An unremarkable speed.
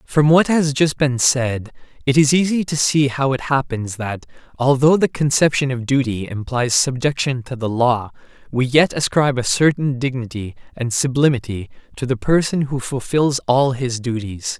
Yes: average, 170 wpm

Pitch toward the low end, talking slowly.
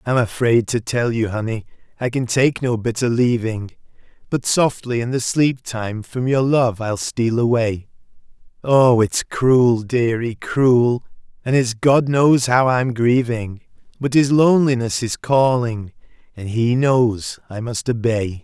No: low, 120 Hz; average, 155 wpm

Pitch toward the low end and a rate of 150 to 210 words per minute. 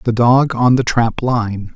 Yes: low, 120 Hz; fast, 205 wpm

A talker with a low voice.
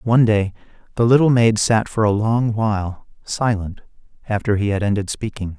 Yes: low, 105 Hz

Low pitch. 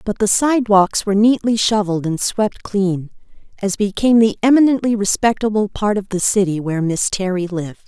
No: high, 205 Hz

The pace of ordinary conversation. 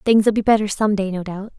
No: fast, 265 wpm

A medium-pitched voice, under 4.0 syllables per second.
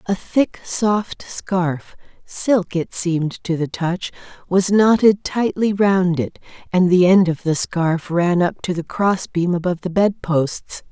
Yes: medium, 180 Hz; 3.7 syllables/s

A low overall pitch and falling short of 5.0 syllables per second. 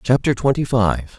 Yes: low, 120 Hz; 4.4 syllables/s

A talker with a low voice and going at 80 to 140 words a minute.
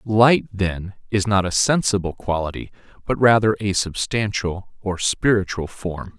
Yes: low, 100 Hz; slow, 135 wpm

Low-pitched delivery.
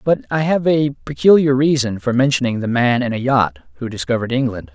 Yes: low, 130 Hz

